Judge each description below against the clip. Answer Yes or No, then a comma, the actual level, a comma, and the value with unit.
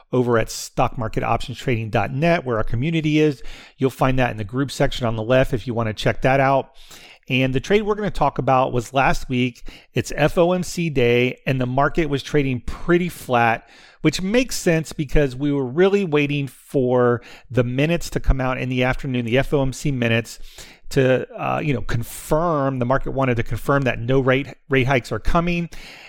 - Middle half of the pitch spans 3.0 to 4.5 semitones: Yes, average, 3.3 semitones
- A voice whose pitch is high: No, low, 135 Hz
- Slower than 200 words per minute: Yes, average, 190 wpm